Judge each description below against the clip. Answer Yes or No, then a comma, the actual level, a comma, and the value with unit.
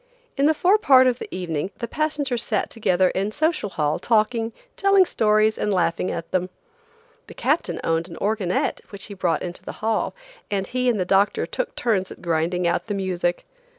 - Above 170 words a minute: Yes, average, 185 wpm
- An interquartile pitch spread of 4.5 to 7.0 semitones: Yes, average, 5.2 semitones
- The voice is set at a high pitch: Yes, high, 205 Hz